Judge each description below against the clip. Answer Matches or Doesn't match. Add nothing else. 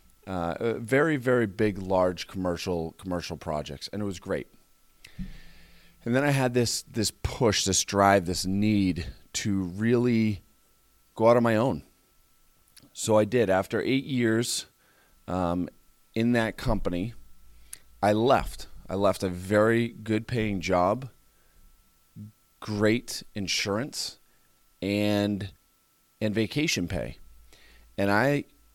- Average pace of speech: Doesn't match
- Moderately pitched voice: Doesn't match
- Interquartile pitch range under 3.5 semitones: Doesn't match